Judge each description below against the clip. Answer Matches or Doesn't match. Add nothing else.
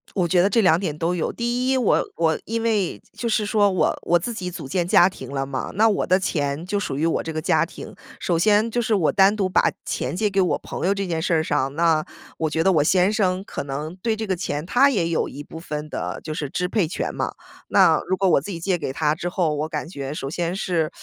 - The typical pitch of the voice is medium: Matches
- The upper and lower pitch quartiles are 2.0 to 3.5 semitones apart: Doesn't match